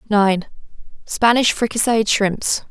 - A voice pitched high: Yes, high, 215 Hz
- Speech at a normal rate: No, slow, 65 wpm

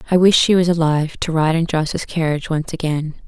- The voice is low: No, medium, 160 Hz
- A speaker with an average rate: No, fast, 220 wpm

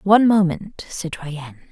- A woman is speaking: Yes, female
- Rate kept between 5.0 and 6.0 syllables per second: Yes, 5.4 syllables/s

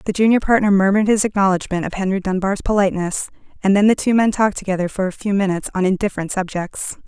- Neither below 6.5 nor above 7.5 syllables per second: Yes, 7.0 syllables/s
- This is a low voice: No, high, 195 Hz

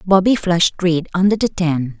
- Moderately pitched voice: Yes, medium, 175 Hz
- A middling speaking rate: Yes, average, 180 wpm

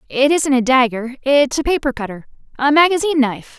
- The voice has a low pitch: No, very high, 270 Hz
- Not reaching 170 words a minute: Yes, average, 150 wpm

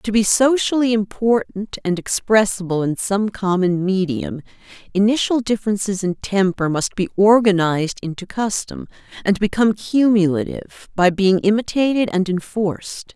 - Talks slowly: Yes, slow, 125 wpm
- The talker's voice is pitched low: No, high, 200 Hz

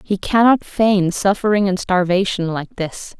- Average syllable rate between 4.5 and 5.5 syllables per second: No, 4.2 syllables/s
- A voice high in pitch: Yes, high, 195 Hz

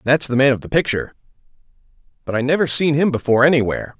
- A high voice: No, low, 135 Hz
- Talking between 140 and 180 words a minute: No, average, 195 wpm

